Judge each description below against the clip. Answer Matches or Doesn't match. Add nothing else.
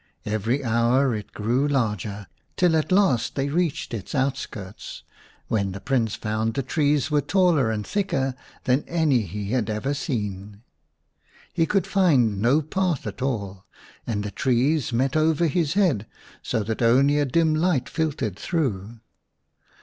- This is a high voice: Doesn't match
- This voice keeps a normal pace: Matches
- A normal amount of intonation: Doesn't match